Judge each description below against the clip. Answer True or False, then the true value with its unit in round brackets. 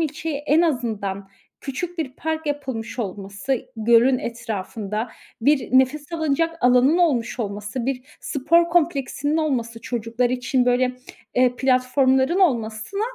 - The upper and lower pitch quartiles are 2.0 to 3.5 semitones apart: False (4.4 semitones)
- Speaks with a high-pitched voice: True (255 Hz)